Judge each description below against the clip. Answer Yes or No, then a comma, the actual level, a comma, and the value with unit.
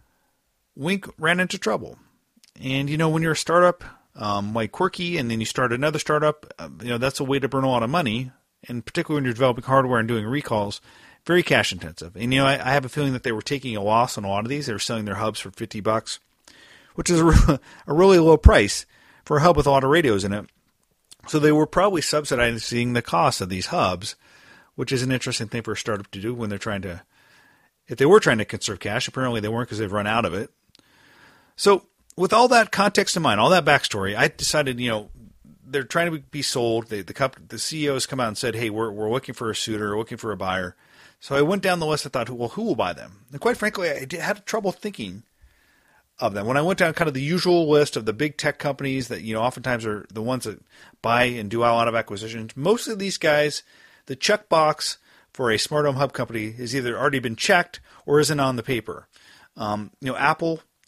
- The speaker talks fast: Yes, fast, 245 wpm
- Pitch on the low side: Yes, low, 130 Hz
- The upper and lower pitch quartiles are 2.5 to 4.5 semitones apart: No, wide, 5.5 semitones